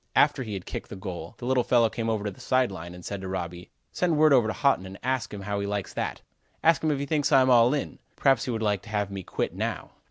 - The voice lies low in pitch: Yes, low, 110 Hz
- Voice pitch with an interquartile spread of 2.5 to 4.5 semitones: No, average, 5.2 semitones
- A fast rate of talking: Yes, fast, 285 wpm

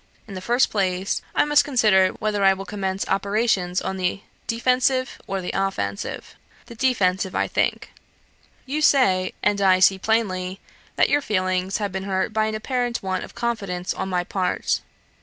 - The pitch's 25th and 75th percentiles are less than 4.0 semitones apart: Yes, average, 3.6 semitones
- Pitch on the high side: Yes, high, 195 Hz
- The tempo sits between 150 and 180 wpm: Yes, average, 170 wpm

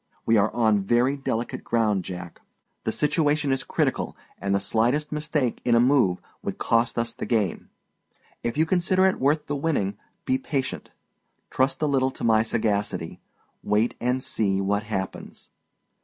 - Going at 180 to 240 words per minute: No, average, 160 wpm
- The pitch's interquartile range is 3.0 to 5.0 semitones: No, wide, 5.5 semitones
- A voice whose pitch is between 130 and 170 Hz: No, low, 120 Hz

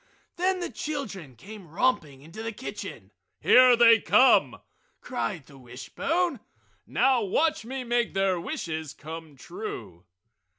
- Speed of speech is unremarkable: No, slow, 125 wpm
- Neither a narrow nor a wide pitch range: No, wide, 8.5 semitones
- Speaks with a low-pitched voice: No, high, 220 Hz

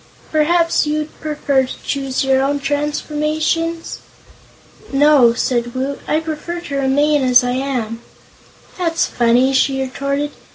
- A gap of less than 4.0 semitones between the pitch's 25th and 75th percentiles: Yes, narrow, 2.5 semitones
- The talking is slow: Yes, slow, 125 wpm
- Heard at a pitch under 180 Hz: No, very high, 280 Hz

